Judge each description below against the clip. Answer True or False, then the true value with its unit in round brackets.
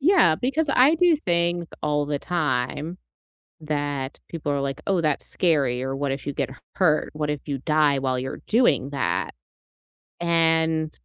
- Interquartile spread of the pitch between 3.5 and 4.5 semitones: True (3.8 semitones)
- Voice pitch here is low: False (150 Hz)